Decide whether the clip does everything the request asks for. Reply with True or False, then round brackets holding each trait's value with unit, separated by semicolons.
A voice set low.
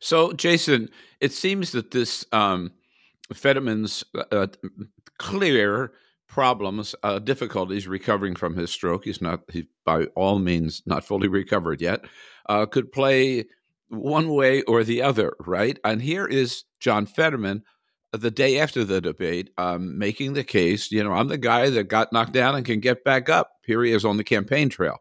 True (115 Hz)